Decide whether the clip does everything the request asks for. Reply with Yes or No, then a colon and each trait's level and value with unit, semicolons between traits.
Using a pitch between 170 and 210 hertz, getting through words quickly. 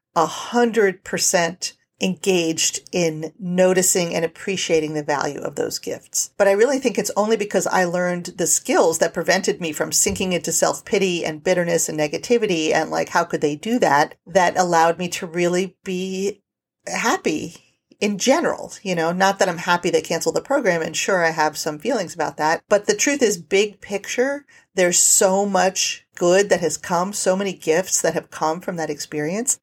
No: medium, 185 Hz; average, 185 wpm